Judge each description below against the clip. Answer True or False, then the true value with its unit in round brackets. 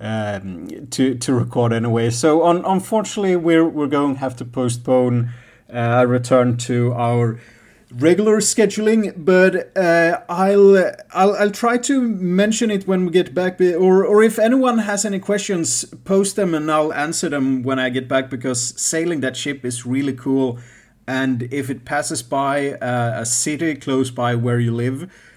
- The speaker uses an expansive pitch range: True (7.0 semitones)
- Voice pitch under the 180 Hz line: True (140 Hz)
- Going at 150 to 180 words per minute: True (170 wpm)